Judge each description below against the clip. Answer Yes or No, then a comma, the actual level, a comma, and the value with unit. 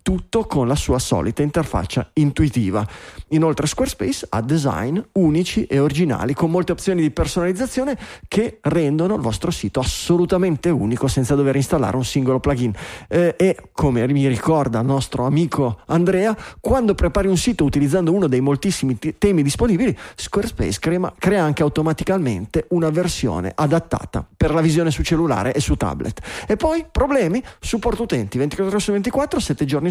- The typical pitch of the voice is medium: Yes, medium, 160 Hz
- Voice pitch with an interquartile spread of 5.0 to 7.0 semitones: Yes, wide, 5.4 semitones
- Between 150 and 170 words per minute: Yes, average, 160 wpm